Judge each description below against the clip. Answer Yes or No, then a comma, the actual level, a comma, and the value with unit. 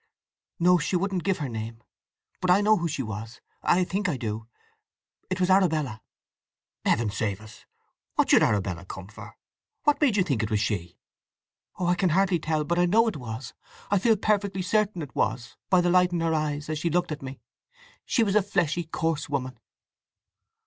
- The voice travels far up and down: Yes, wide, 7.7 semitones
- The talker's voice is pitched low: No, medium, 165 Hz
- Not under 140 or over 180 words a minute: No, average, 190 wpm